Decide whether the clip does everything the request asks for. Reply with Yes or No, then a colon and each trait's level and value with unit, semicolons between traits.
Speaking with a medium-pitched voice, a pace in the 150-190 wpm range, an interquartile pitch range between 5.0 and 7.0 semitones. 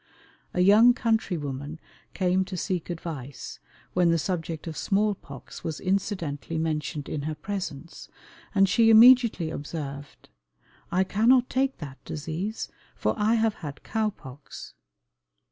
No: medium, 175 Hz; slow, 135 wpm; wide, 5.6 semitones